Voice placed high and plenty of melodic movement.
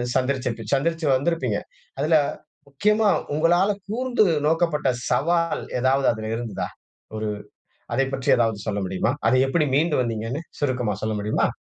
No: low, 135 Hz; wide, 6.2 semitones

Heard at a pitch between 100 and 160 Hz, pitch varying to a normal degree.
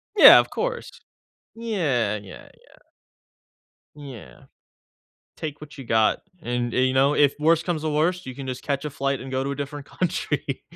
Yes: medium, 140 Hz; average, 3.1 semitones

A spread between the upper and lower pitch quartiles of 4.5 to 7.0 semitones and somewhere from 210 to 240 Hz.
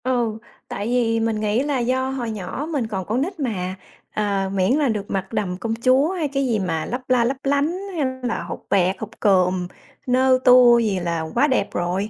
Yes: average, 4.8 semitones; high, 230 Hz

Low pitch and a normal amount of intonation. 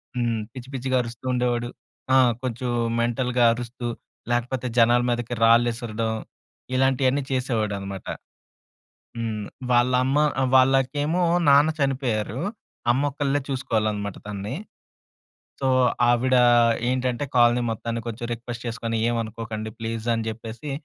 No: low, 120 Hz; narrow, 2.2 semitones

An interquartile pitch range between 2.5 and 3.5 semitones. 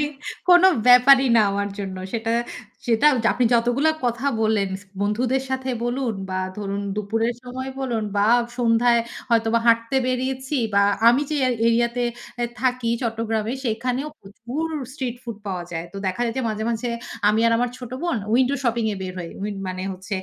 Yes: average, 2.8 semitones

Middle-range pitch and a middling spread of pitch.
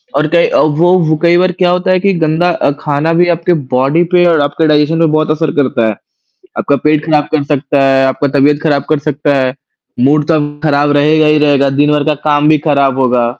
No: medium, 150 Hz; narrow, 2.1 semitones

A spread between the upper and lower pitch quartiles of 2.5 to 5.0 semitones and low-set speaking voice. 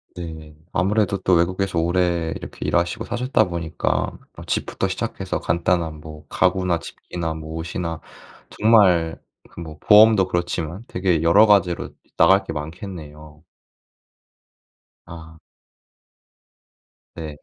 Yes: average, 2.8 semitones; very low, 85 Hz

